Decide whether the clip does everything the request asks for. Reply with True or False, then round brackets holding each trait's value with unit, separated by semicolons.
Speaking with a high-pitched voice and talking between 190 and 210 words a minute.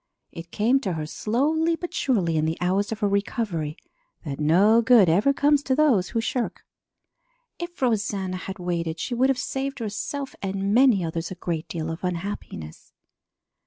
False (200 Hz; 170 wpm)